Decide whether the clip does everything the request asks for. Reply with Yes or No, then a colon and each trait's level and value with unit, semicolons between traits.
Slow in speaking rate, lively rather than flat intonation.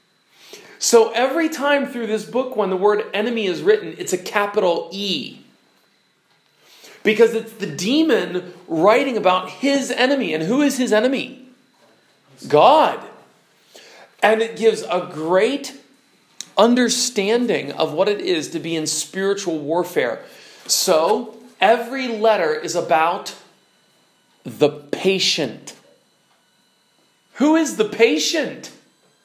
Yes: slow, 115 wpm; wide, 5.7 semitones